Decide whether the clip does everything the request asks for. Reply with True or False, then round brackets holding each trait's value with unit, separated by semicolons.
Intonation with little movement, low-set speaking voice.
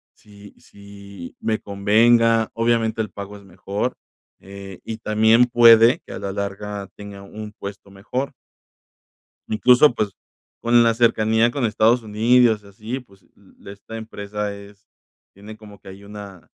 True (2.3 semitones; 105 Hz)